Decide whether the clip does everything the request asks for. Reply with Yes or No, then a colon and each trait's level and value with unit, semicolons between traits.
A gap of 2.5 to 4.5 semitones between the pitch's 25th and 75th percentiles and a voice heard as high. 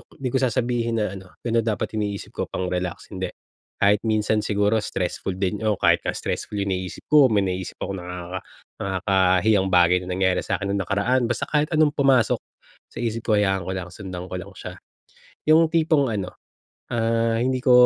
No: average, 3.9 semitones; low, 105 Hz